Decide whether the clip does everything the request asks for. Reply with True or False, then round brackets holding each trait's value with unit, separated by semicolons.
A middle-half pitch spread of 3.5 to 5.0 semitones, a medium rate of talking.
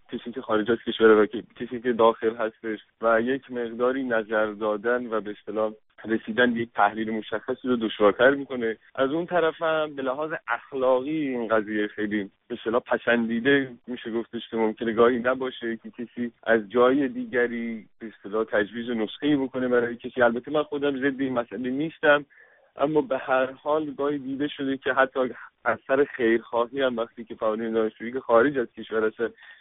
False (2.9 semitones; 170 wpm)